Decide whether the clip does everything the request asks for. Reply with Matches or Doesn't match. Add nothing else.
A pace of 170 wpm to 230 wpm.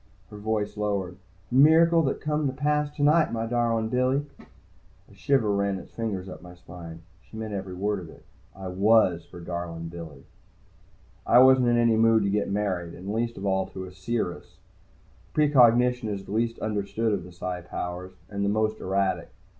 Matches